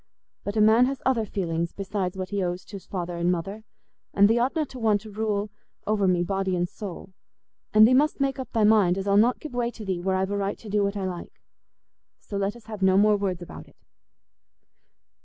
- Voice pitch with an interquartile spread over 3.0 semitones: No, average, 2.7 semitones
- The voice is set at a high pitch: Yes, high, 200 Hz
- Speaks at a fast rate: Yes, fast, 230 wpm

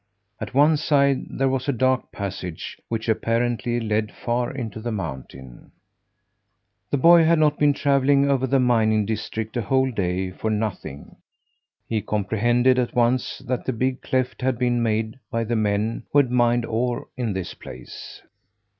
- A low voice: Yes, low, 120 Hz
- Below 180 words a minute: Yes, average, 165 wpm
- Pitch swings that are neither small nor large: Yes, average, 3.2 semitones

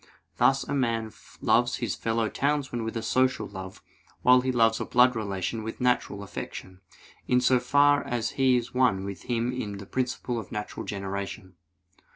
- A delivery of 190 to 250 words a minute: No, average, 175 wpm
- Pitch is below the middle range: Yes, low, 115 Hz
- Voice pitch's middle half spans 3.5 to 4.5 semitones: Yes, average, 3.8 semitones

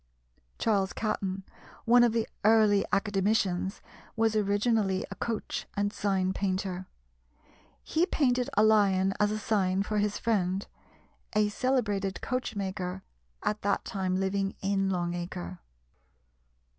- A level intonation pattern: Yes, narrow, 2.2 semitones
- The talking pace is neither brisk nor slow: No, slow, 120 wpm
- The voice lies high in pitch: Yes, high, 200 Hz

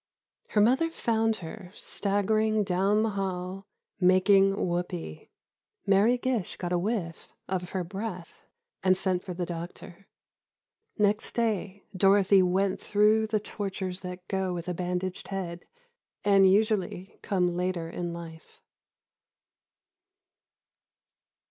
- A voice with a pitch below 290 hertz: Yes, high, 190 Hz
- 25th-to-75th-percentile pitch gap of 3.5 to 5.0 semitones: No, narrow, 2.5 semitones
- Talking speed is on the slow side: Yes, slow, 115 wpm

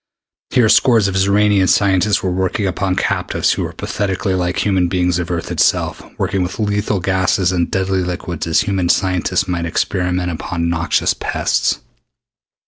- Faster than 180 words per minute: No, average, 155 wpm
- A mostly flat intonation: Yes, narrow, 1.7 semitones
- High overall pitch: No, very low, 95 Hz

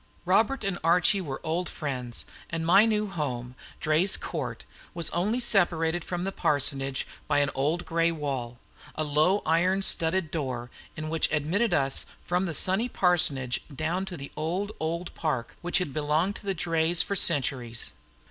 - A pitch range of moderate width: Yes, average, 4.1 semitones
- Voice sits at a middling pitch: Yes, medium, 165 Hz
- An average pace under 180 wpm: Yes, average, 165 wpm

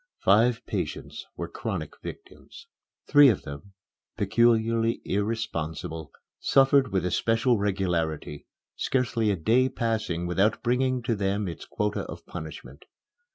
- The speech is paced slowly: Yes, slow, 115 wpm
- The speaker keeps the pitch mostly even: No, average, 4.6 semitones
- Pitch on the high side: No, low, 110 Hz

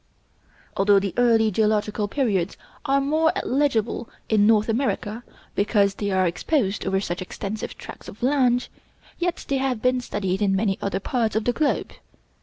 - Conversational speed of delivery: Yes, average, 160 wpm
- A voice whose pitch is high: Yes, high, 220 Hz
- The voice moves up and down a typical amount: Yes, average, 4.0 semitones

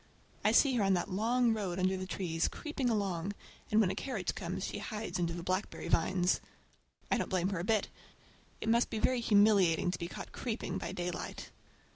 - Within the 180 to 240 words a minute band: Yes, average, 200 wpm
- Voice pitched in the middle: No, high, 195 Hz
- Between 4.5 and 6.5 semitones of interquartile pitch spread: No, average, 3.7 semitones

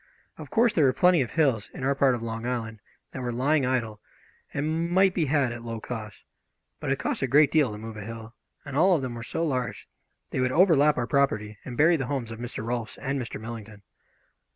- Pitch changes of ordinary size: Yes, average, 4.5 semitones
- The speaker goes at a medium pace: No, fast, 230 wpm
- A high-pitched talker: No, low, 130 Hz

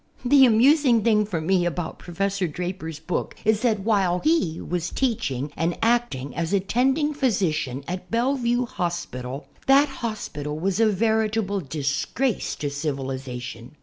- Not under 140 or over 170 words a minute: Yes, average, 145 wpm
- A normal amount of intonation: No, wide, 6.9 semitones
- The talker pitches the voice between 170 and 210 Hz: Yes, high, 190 Hz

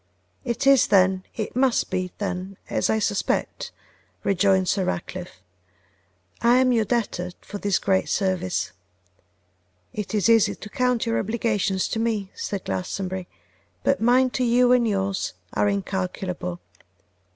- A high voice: Yes, high, 200 Hz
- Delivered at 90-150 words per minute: Yes, average, 140 wpm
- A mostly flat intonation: No, average, 3.8 semitones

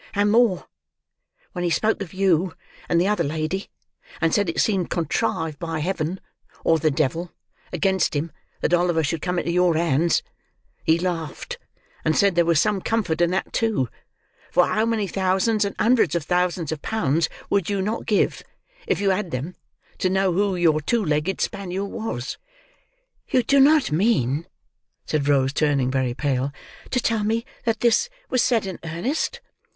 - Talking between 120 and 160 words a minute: No, average, 170 wpm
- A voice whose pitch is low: No, medium, 180 Hz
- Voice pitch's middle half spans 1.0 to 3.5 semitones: No, average, 4.4 semitones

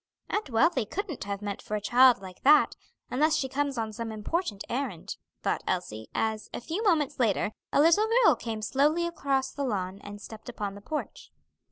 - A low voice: No, high, 245 Hz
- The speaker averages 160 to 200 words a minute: Yes, average, 190 wpm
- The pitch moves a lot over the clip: Yes, wide, 6.4 semitones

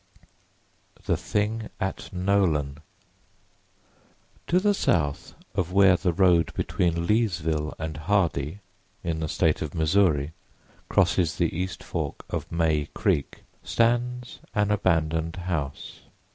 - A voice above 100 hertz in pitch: No, very low, 85 Hz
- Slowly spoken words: Yes, slow, 115 wpm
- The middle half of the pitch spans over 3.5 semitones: Yes, average, 4.2 semitones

